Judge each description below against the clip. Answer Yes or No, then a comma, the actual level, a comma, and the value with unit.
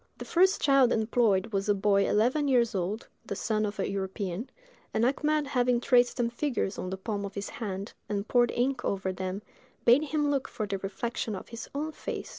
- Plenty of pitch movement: No, average, 4.3 semitones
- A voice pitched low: No, high, 225 Hz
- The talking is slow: No, fast, 205 wpm